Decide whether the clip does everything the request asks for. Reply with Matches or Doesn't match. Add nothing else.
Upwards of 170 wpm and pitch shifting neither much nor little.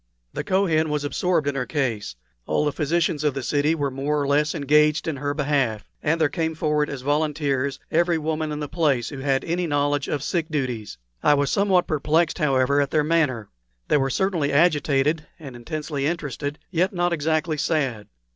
Doesn't match